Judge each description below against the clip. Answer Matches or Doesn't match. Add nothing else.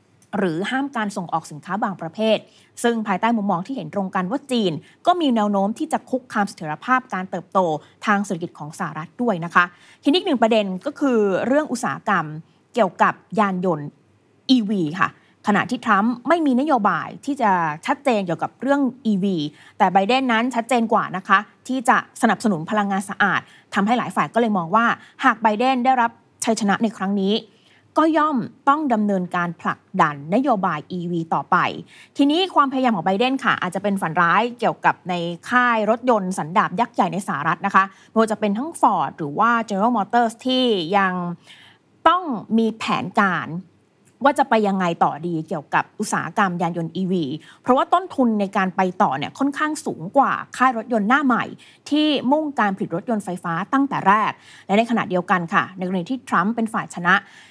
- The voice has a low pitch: Doesn't match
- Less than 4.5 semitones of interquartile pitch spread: Doesn't match